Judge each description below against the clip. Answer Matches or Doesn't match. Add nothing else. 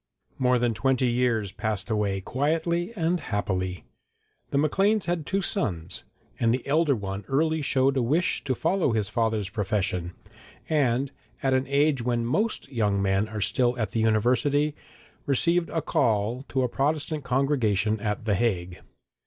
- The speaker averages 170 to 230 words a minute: Doesn't match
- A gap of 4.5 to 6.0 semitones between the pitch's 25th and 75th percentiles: Matches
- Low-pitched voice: Matches